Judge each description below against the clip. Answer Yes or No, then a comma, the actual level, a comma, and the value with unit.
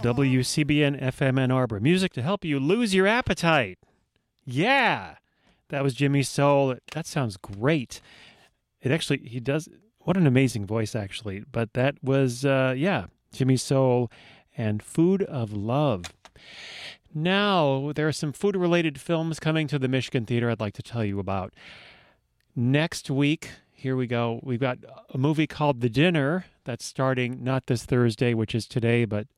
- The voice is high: No, low, 135 Hz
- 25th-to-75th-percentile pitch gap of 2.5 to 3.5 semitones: No, average, 4.1 semitones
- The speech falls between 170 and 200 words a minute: No, average, 160 wpm